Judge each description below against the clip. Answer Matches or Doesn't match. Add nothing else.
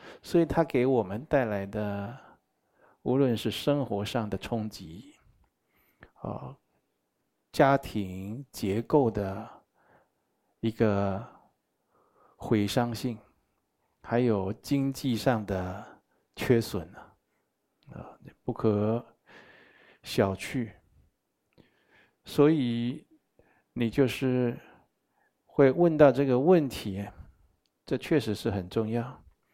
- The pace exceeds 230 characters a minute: Doesn't match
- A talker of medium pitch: Doesn't match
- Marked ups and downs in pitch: Doesn't match